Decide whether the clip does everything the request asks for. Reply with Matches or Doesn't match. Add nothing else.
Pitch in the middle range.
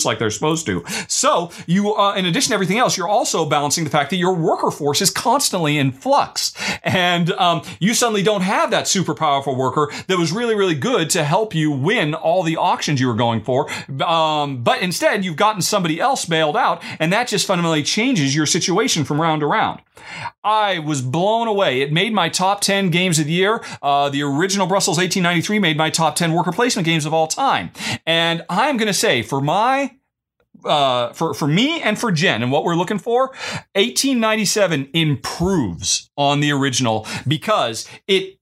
Matches